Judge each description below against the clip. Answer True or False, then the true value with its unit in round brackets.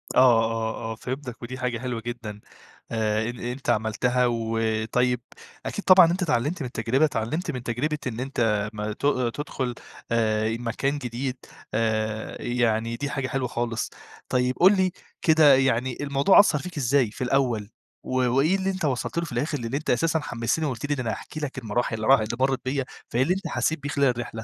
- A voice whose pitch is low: True (125 Hz)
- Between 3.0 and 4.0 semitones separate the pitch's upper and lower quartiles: True (3.7 semitones)